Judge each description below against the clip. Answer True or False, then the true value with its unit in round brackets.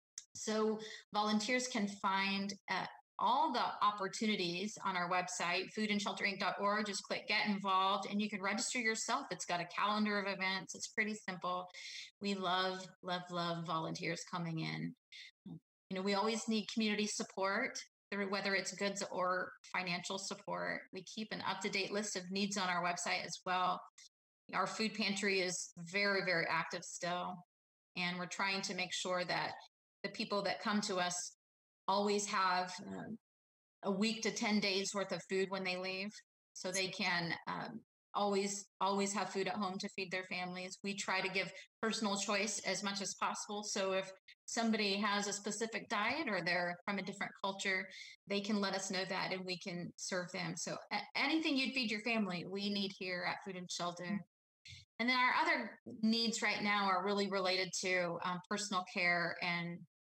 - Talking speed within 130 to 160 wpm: False (175 wpm)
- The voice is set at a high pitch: True (195 Hz)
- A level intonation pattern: True (2.2 semitones)